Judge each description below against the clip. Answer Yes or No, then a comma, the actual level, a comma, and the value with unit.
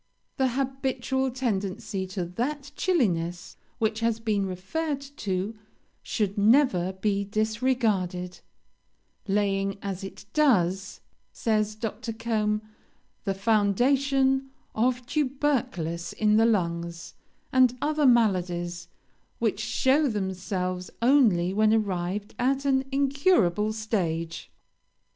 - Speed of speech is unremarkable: No, slow, 100 wpm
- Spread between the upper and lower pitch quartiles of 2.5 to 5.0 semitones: No, wide, 5.4 semitones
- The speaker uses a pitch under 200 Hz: No, high, 215 Hz